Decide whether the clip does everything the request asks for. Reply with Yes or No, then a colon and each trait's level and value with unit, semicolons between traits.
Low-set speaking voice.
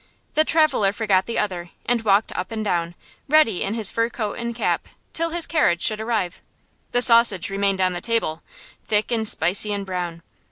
No: high, 210 Hz